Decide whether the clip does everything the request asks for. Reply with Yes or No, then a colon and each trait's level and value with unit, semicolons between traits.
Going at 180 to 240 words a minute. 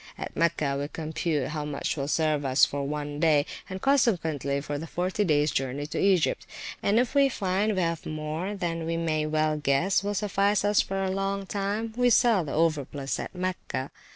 Yes: average, 195 wpm